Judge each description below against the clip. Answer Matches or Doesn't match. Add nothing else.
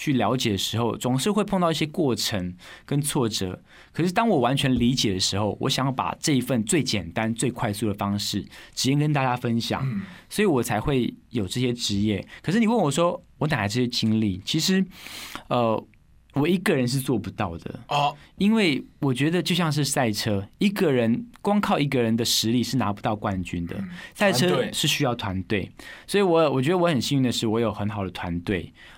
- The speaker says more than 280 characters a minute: Matches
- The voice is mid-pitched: Doesn't match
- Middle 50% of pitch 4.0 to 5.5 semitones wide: Doesn't match